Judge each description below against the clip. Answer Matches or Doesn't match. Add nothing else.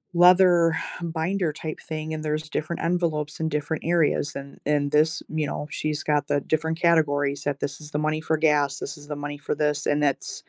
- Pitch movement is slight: Matches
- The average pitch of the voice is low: Doesn't match